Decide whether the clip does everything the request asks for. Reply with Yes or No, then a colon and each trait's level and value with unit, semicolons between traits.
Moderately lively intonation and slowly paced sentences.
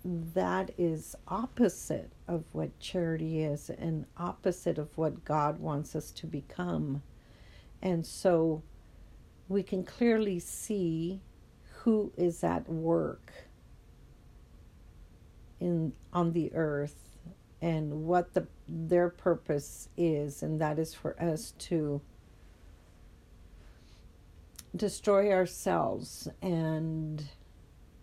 Yes: average, 3.7 semitones; slow, 95 wpm